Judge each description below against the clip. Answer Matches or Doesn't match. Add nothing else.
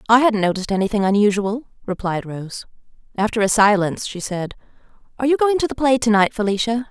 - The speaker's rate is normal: Matches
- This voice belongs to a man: Doesn't match